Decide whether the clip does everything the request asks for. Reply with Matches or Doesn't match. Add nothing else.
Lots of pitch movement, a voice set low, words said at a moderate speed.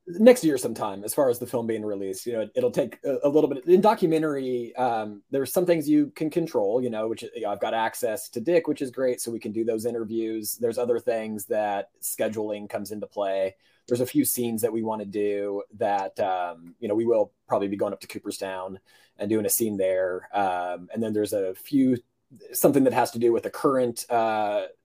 Doesn't match